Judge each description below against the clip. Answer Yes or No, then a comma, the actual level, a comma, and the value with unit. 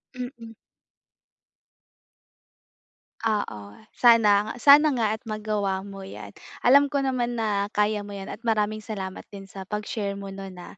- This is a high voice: Yes, high, 210 Hz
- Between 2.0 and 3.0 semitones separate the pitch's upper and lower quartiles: Yes, narrow, 2.6 semitones